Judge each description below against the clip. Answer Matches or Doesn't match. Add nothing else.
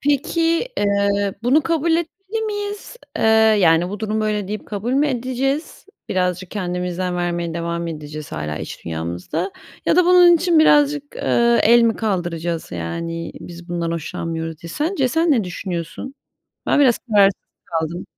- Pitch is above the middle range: Matches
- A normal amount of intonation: Doesn't match